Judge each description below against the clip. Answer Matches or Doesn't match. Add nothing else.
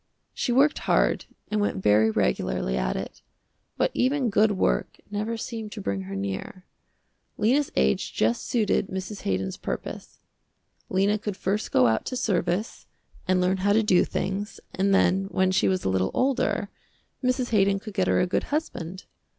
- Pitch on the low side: Doesn't match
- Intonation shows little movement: Doesn't match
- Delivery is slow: Doesn't match